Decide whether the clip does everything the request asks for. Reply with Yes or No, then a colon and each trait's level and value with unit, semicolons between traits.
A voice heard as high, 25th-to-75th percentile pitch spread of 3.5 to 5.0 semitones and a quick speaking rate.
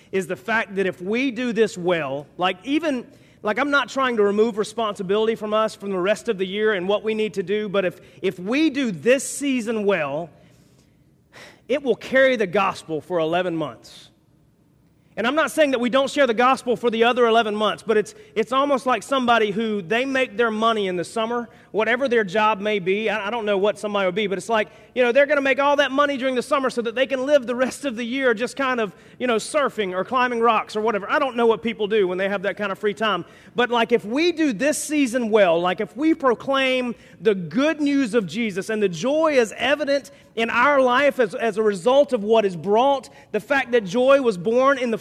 Yes: high, 230 Hz; average, 3.8 semitones; fast, 240 wpm